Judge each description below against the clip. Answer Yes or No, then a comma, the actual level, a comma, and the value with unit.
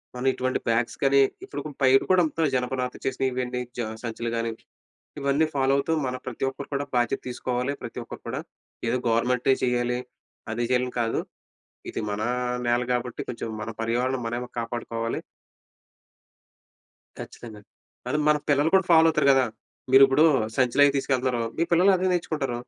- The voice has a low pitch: Yes, low, 125 Hz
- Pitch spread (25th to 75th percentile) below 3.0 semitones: Yes, narrow, 2.5 semitones